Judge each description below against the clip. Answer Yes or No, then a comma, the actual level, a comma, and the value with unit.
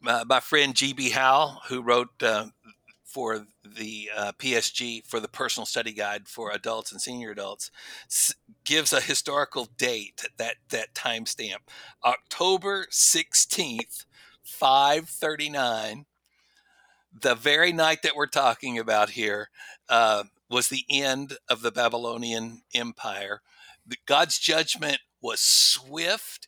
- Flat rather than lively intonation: No, average, 4.1 semitones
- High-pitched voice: No, low, 125 Hz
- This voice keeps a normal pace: No, slow, 125 wpm